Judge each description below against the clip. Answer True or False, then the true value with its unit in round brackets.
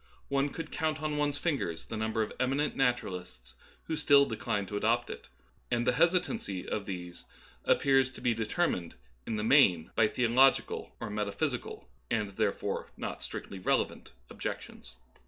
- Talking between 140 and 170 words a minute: True (155 wpm)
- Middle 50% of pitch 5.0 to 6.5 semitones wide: True (5.6 semitones)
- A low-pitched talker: True (115 Hz)